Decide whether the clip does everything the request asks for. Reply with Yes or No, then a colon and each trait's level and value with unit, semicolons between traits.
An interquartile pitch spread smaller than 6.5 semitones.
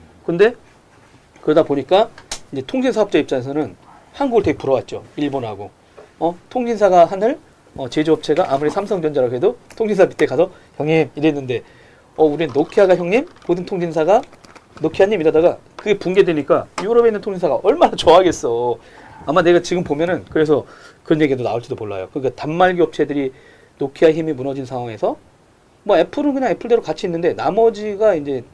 Yes: wide, 5.8 semitones